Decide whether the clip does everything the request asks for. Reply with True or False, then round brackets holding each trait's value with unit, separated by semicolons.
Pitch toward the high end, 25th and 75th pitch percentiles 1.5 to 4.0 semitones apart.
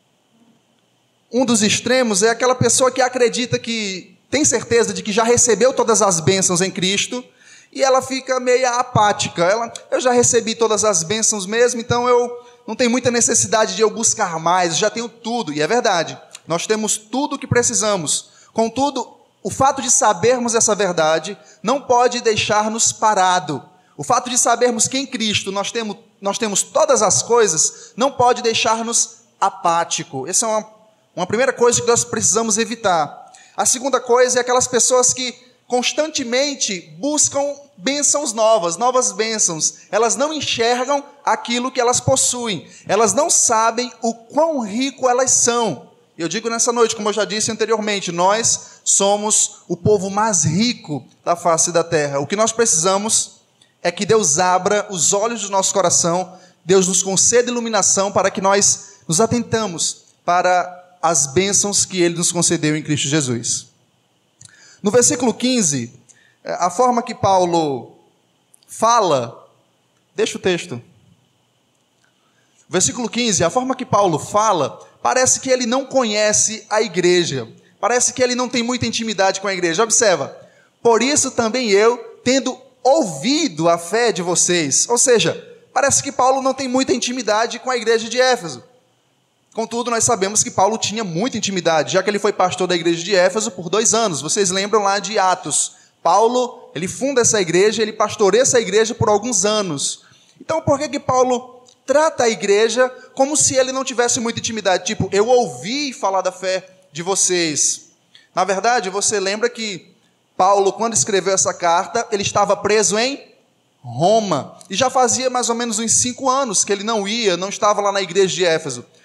False (220 Hz; 4.5 semitones)